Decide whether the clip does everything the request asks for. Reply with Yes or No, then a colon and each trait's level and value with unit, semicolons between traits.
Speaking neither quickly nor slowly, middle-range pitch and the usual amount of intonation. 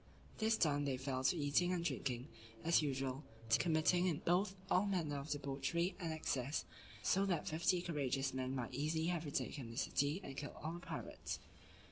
Yes: average, 175 wpm; medium, 150 Hz; average, 4.2 semitones